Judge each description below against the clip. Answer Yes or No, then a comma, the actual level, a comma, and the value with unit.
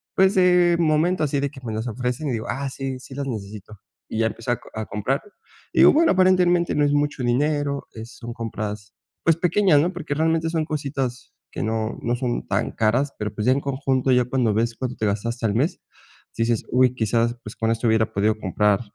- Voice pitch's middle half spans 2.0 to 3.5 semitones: No, average, 4.7 semitones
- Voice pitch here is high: No, low, 125 Hz